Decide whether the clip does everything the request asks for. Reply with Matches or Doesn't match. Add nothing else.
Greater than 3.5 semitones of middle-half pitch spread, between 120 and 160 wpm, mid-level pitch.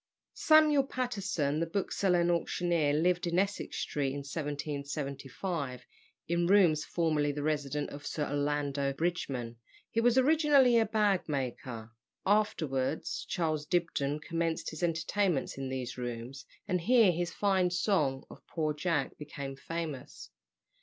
Matches